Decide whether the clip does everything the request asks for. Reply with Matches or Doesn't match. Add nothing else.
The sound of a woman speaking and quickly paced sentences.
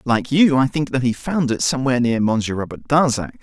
Doesn't match